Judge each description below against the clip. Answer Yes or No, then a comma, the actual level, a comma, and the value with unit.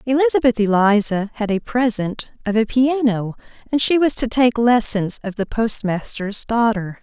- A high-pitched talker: Yes, high, 225 Hz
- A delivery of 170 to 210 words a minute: No, average, 155 wpm